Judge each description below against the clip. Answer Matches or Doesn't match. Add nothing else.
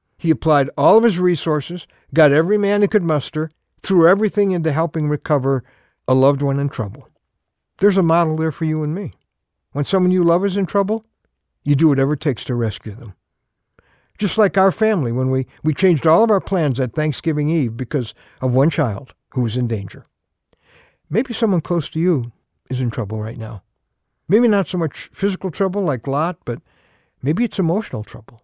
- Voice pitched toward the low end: Doesn't match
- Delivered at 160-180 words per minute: Doesn't match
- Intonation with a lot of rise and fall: Matches